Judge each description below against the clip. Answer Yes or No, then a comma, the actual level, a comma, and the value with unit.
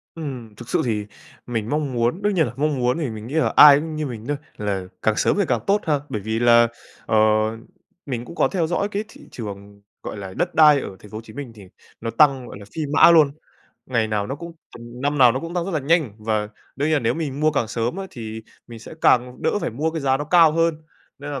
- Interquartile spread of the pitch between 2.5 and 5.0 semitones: No, wide, 5.5 semitones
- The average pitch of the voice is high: No, low, 130 Hz